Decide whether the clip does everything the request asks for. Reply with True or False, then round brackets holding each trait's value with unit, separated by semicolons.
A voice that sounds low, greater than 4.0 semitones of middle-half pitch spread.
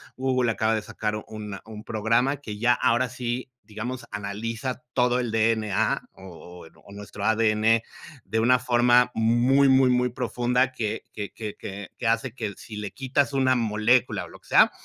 False (115 Hz; 2.7 semitones)